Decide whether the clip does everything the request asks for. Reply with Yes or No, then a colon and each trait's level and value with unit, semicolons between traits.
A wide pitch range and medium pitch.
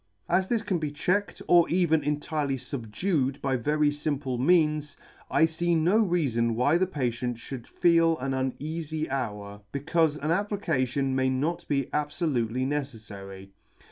No: average, 4.3 semitones; medium, 145 Hz